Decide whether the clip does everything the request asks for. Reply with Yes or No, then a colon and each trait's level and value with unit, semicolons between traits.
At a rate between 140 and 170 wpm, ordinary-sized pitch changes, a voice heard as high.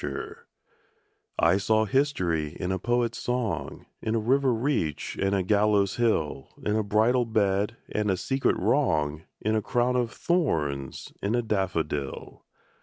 No: average, 150 wpm; average, 5.0 semitones; low, 105 Hz